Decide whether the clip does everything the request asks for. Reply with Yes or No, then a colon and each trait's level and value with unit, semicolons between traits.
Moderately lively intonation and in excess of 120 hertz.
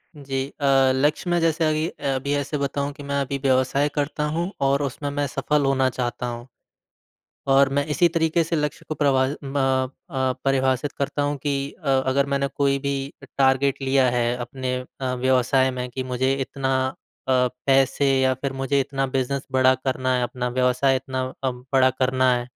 No: narrow, 1.5 semitones; low, 135 Hz